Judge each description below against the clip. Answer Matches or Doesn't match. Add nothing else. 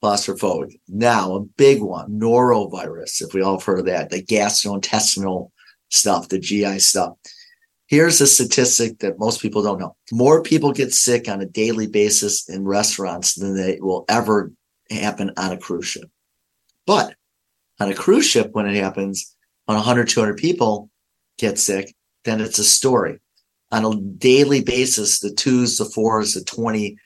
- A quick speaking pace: Doesn't match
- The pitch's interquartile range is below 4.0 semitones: Matches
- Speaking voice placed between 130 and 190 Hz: Doesn't match